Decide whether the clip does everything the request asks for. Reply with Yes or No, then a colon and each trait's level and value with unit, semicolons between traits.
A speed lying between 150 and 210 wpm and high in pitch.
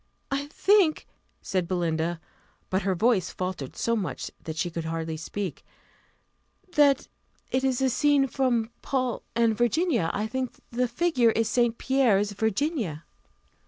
No: average, 140 wpm; high, 230 Hz